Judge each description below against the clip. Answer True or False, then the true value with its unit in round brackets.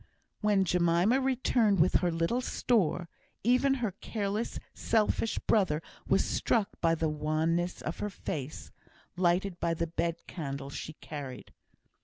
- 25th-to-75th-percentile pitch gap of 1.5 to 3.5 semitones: False (4.5 semitones)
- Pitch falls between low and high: True (175 Hz)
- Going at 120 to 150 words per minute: True (135 wpm)